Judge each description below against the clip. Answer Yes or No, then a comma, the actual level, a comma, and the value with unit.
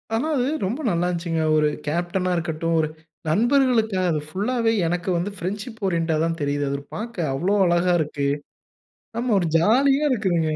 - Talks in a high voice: No, medium, 180 Hz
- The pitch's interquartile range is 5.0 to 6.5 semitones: Yes, average, 5.3 semitones